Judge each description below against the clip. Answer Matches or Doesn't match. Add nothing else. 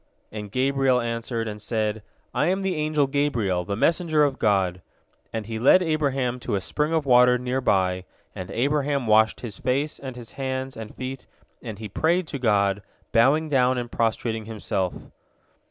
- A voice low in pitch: Matches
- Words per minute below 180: Matches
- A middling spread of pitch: Matches